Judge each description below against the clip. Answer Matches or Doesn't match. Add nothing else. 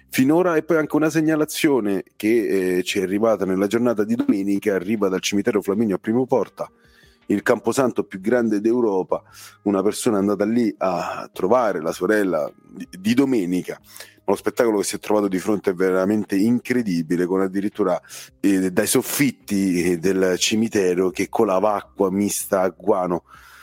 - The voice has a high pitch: Doesn't match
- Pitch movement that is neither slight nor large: Matches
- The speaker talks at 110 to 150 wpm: Doesn't match